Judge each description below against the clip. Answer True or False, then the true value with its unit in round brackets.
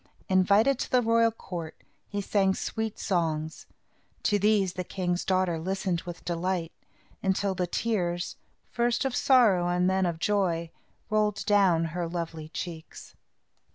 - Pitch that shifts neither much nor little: True (3.2 semitones)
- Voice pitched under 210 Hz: True (185 Hz)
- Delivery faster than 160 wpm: False (140 wpm)